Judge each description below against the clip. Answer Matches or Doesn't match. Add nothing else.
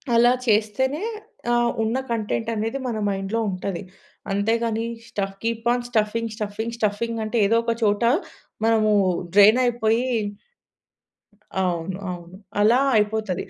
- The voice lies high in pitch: Matches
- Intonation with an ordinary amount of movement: Doesn't match